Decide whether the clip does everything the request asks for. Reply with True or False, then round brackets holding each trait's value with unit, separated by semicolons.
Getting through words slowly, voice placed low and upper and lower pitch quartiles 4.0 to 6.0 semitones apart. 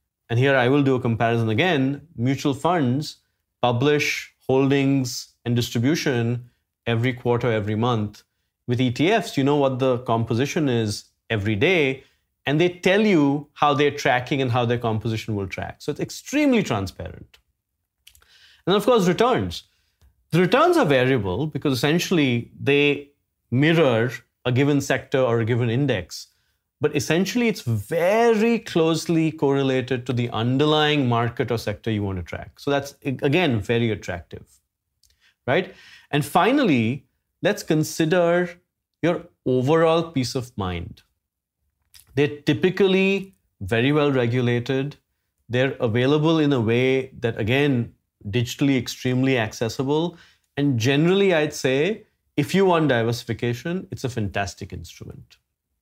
True (130 wpm; 130 Hz; 4.4 semitones)